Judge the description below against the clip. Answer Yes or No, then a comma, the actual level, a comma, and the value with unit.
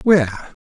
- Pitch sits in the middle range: Yes, medium, 150 Hz